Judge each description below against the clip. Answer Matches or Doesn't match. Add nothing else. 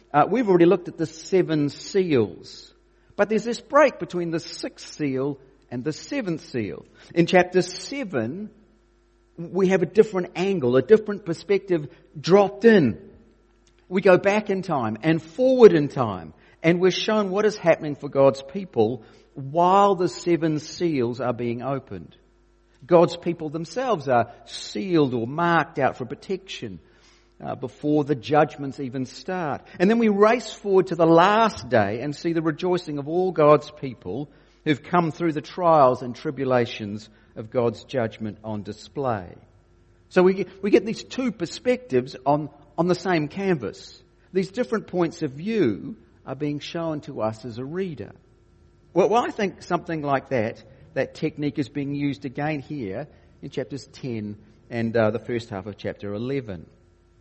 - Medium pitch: Matches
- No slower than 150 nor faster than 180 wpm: Matches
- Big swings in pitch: Matches